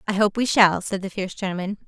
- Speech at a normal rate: No, fast, 255 wpm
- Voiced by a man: No, female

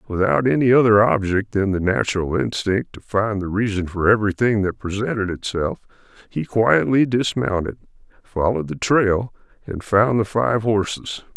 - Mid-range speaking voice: No, low, 105 Hz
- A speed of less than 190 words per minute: Yes, average, 150 wpm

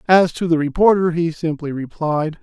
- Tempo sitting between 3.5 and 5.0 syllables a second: Yes, 4.9 syllables/s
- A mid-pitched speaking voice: Yes, medium, 165 Hz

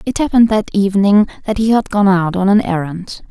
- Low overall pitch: No, high, 200 Hz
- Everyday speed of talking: No, fast, 220 wpm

